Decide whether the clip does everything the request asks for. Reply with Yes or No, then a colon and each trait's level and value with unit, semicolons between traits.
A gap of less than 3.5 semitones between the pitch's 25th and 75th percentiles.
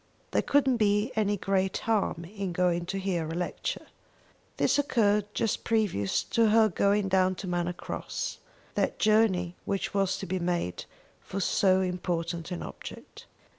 Yes: average, 3.0 semitones